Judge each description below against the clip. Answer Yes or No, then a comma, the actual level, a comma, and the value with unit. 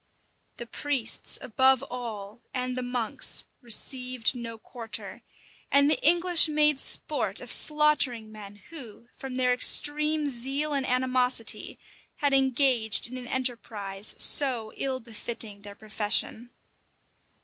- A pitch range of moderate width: Yes, average, 3.3 semitones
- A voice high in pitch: Yes, very high, 250 Hz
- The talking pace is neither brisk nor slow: No, slow, 120 wpm